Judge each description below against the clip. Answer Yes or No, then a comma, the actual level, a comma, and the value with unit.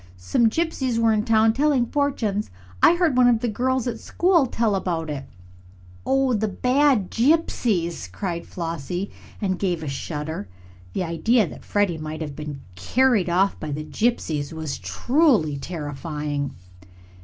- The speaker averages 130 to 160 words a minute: Yes, average, 150 wpm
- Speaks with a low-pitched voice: No, high, 200 Hz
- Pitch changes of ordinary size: No, wide, 7.7 semitones